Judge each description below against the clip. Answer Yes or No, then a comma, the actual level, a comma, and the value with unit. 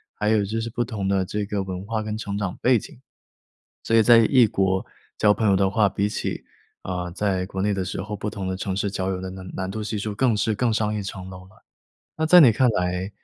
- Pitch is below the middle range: Yes, low, 100 Hz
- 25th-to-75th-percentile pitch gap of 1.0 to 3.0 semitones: Yes, narrow, 2.5 semitones